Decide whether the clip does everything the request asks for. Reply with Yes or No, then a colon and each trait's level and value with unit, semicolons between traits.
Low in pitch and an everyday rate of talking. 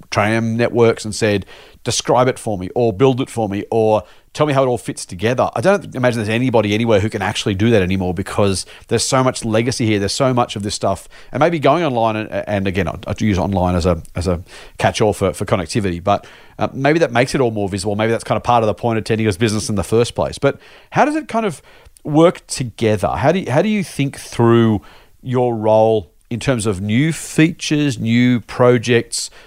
No: low, 115 Hz; fast, 230 wpm